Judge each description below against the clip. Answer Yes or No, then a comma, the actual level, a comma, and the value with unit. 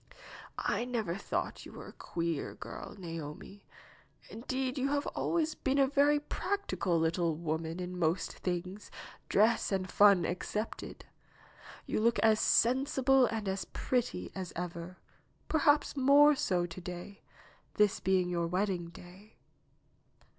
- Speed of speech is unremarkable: No, slow, 130 wpm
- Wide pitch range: Yes, wide, 6.7 semitones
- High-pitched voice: Yes, high, 195 Hz